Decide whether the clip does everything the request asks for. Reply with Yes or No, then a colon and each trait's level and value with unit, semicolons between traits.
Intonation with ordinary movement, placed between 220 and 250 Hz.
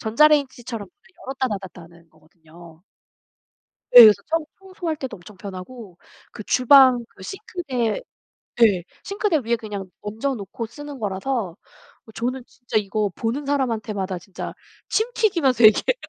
No: wide, 6.1 semitones; high, 230 Hz